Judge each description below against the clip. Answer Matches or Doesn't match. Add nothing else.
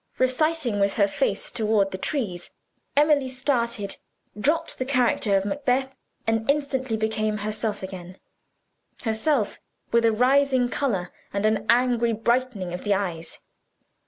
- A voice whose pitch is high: Matches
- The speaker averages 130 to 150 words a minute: Matches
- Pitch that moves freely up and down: Doesn't match